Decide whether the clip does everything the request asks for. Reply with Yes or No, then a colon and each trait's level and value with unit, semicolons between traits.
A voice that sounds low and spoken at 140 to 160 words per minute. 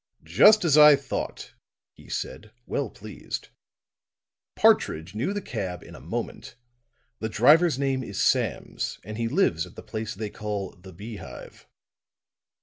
Yes: low, 110 Hz; average, 145 wpm